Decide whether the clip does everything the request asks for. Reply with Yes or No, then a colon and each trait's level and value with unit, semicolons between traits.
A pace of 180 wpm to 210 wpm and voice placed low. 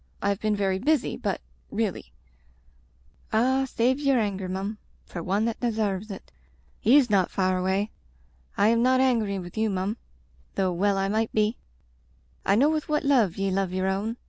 No: average, 185 wpm; high, 205 Hz